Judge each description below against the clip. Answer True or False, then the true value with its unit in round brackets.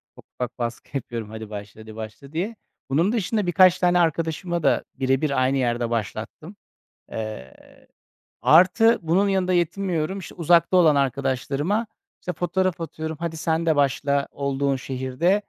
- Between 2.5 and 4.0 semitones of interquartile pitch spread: False (5.4 semitones)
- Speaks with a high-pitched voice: False (155 Hz)